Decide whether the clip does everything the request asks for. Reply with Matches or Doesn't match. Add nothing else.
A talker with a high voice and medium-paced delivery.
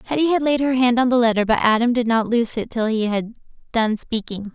Doesn't match